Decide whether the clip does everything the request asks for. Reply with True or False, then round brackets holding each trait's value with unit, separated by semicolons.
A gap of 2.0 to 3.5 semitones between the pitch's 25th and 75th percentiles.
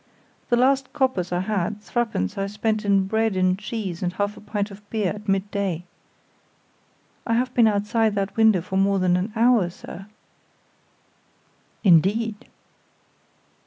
True (2.8 semitones)